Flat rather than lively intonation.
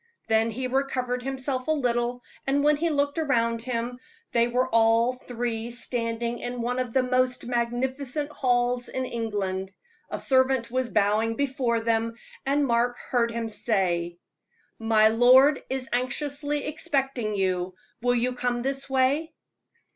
Yes: narrow, 2.3 semitones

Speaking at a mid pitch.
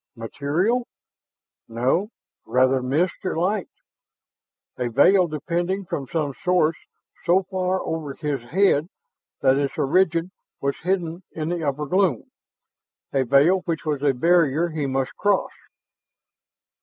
Yes: medium, 160 Hz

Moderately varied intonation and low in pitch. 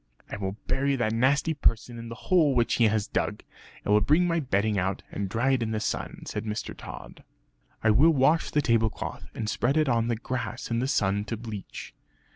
Yes: average, 4.0 semitones; low, 115 Hz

